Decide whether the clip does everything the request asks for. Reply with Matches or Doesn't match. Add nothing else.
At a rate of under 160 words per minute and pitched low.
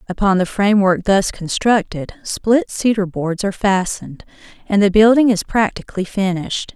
Doesn't match